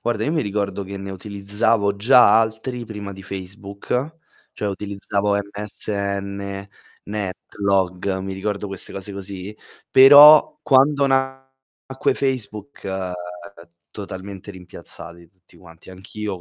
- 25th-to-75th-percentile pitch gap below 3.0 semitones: Yes, narrow, 2.6 semitones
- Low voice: Yes, low, 100 Hz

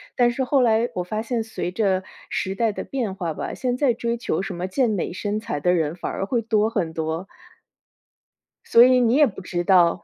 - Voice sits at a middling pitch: No, high, 215 Hz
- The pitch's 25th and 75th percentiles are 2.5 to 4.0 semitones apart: No, average, 4.7 semitones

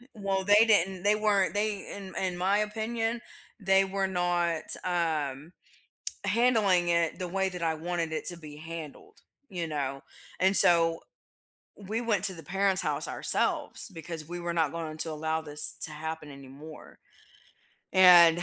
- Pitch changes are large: No, average, 3.5 semitones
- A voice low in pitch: No, medium, 175 Hz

